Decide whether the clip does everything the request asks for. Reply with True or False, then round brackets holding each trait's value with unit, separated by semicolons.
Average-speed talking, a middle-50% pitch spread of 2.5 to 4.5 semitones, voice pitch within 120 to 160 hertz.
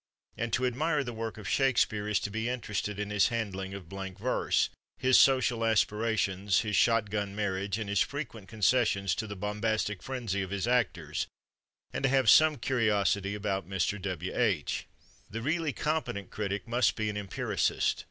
False (170 wpm; 3.3 semitones; 105 Hz)